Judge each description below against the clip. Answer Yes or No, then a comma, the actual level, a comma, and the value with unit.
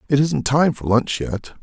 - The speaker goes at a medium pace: No, fast, 220 wpm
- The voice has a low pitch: Yes, low, 130 Hz